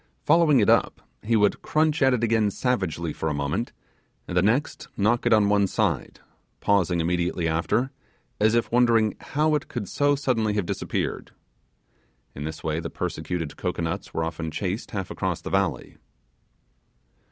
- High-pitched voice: No, low, 105 Hz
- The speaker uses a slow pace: No, average, 165 wpm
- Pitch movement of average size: No, wide, 6.1 semitones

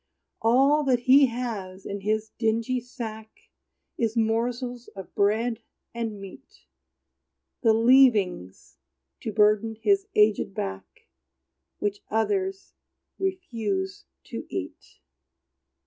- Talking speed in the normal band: No, slow, 100 wpm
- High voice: Yes, high, 225 Hz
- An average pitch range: Yes, average, 3.1 semitones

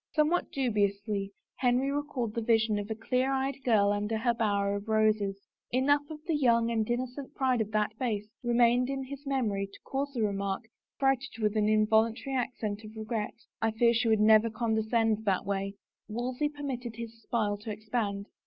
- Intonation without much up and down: No, average, 3.2 semitones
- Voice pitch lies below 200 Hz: No, high, 225 Hz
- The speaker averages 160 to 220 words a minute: Yes, average, 185 wpm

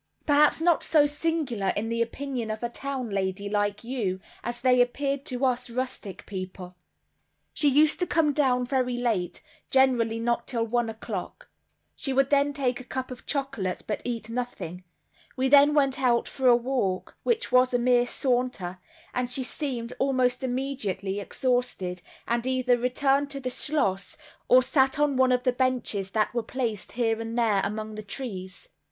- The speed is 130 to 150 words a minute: No, average, 170 wpm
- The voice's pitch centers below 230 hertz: No, very high, 250 Hz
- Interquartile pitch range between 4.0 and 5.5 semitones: No, average, 3.4 semitones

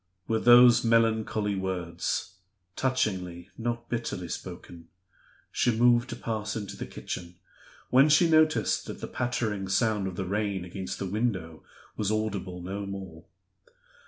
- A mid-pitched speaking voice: No, low, 105 Hz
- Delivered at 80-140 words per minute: Yes, slow, 135 wpm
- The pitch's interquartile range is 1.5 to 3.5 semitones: No, average, 4.1 semitones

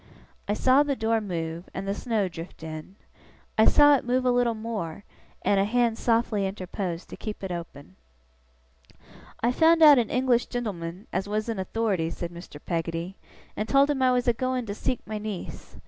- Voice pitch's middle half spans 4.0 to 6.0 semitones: Yes, average, 5.3 semitones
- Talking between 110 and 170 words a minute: No, average, 190 wpm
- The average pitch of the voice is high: Yes, high, 215 Hz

